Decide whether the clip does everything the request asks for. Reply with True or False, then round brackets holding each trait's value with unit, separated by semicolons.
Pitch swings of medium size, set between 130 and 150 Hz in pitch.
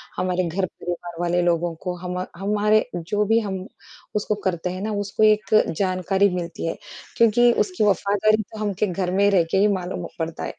False (3.0 semitones; 190 Hz)